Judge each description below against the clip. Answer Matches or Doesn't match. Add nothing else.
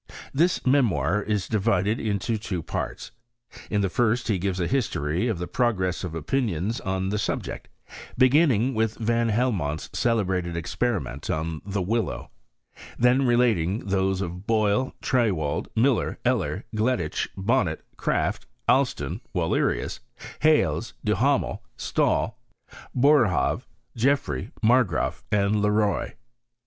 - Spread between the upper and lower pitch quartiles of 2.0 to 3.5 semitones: Doesn't match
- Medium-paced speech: Doesn't match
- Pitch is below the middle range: Matches